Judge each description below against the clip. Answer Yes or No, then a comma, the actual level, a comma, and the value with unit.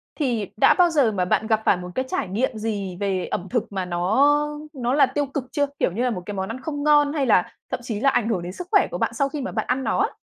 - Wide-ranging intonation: Yes, wide, 6.3 semitones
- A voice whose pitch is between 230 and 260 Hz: Yes, high, 240 Hz